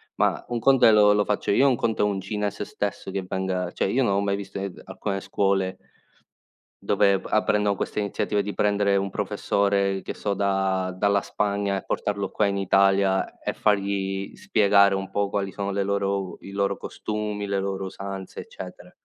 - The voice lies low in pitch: Yes, low, 100 Hz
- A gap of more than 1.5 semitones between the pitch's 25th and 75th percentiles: No, narrow, 0.9 semitones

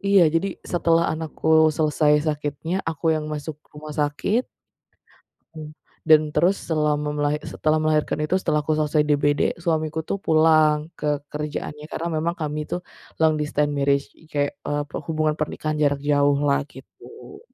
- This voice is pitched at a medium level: Yes, medium, 155 Hz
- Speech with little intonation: Yes, narrow, 1.3 semitones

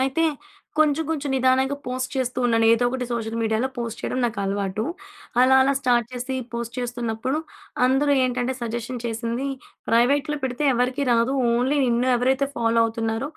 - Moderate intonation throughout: No, narrow, 2.2 semitones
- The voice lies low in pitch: No, high, 245 Hz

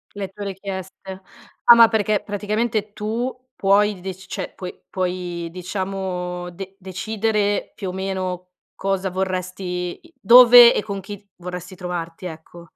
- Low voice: No, high, 190 Hz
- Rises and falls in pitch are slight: Yes, narrow, 2.3 semitones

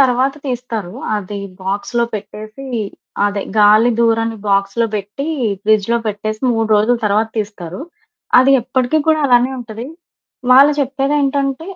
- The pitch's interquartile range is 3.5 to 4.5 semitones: Yes, average, 3.9 semitones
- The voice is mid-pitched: No, high, 230 Hz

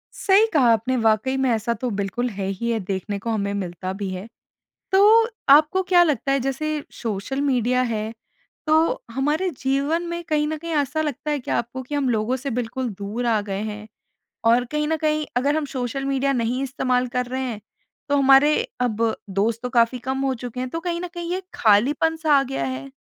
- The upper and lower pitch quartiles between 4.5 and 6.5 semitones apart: Yes, average, 4.9 semitones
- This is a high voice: Yes, very high, 255 Hz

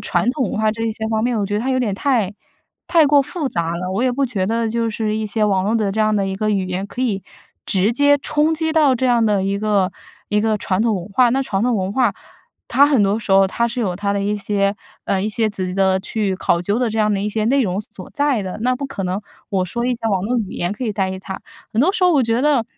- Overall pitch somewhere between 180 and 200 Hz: No, high, 215 Hz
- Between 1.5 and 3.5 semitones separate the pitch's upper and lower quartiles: No, average, 3.9 semitones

